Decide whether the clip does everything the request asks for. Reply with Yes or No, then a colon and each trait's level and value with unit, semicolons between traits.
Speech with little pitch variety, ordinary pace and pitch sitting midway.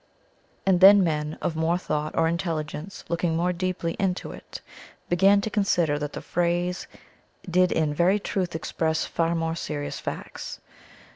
Yes: narrow, 2.3 semitones; average, 150 wpm; medium, 170 Hz